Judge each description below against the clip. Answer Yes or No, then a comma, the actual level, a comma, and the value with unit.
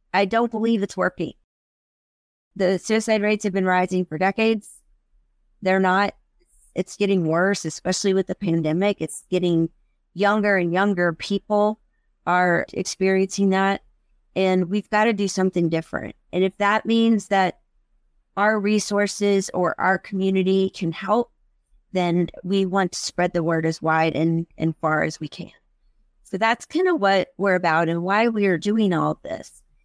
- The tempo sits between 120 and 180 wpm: Yes, average, 160 wpm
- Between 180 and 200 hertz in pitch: Yes, high, 190 Hz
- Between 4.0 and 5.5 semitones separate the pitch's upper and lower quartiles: No, average, 2.7 semitones